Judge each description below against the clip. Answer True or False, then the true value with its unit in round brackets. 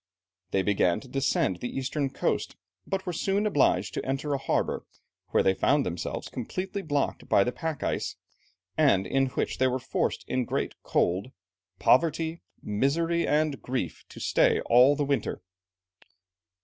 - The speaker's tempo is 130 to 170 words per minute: True (160 wpm)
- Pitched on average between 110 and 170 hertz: True (135 Hz)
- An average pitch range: True (4.5 semitones)